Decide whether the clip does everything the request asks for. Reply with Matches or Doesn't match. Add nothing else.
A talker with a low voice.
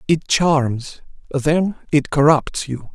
Doesn't match